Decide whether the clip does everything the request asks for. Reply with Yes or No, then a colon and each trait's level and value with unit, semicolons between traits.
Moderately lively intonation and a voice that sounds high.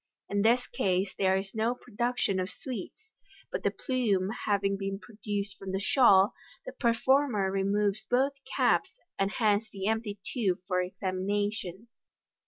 Yes: average, 3.3 semitones; high, 205 Hz